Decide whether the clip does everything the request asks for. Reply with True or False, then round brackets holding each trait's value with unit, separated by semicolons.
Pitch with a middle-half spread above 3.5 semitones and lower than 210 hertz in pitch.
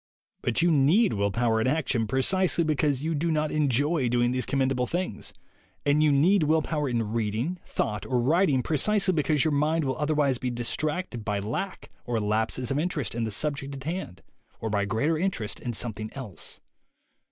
True (4.9 semitones; 140 Hz)